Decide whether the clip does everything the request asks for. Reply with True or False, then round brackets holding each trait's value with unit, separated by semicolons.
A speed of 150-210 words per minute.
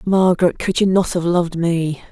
True (200 wpm)